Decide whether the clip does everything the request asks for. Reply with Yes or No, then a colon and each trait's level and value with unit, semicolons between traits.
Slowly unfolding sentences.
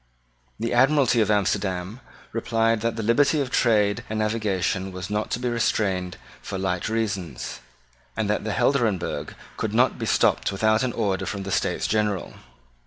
No: average, 165 wpm